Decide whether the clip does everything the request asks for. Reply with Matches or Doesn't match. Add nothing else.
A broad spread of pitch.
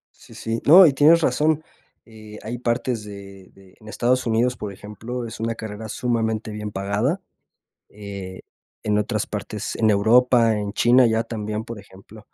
Doesn't match